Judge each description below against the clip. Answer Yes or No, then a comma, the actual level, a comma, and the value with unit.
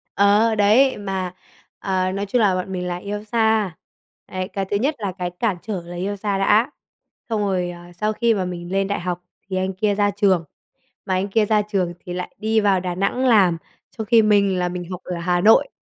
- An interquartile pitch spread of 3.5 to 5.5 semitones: No, narrow, 2.6 semitones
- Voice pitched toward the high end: Yes, high, 195 Hz